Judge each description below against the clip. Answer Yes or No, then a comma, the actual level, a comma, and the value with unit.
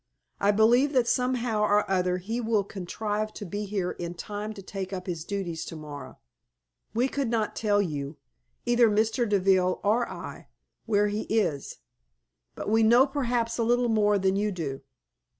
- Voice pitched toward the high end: Yes, high, 210 Hz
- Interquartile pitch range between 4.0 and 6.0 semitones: No, average, 3.4 semitones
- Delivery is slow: No, average, 170 wpm